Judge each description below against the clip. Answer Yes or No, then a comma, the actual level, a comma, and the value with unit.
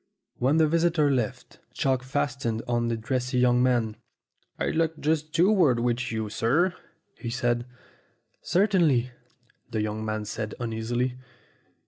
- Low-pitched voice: Yes, low, 125 Hz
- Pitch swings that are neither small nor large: Yes, average, 4.5 semitones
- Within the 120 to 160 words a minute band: Yes, average, 140 wpm